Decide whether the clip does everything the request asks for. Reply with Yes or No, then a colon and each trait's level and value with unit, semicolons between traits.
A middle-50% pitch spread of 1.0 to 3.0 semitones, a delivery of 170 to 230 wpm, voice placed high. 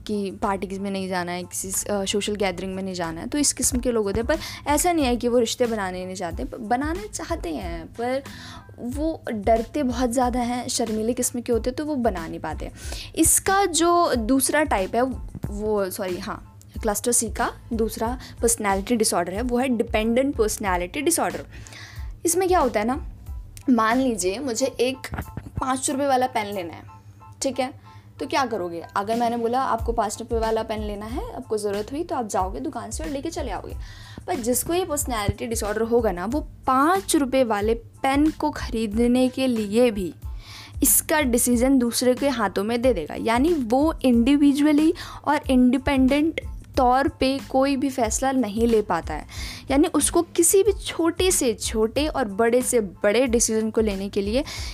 No: average, 4.4 semitones; average, 185 wpm; high, 245 Hz